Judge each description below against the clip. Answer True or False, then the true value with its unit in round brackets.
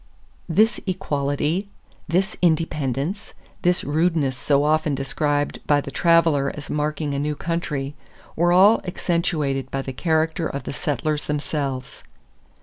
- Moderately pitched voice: True (150 Hz)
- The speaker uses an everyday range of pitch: True (3.2 semitones)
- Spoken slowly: True (130 wpm)